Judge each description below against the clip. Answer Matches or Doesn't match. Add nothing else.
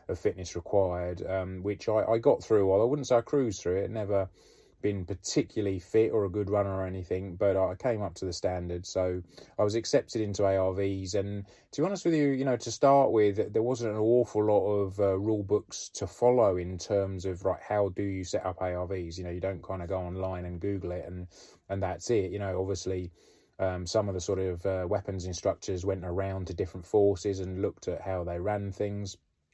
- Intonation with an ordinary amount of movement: Doesn't match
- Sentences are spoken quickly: Matches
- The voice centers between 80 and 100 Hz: Matches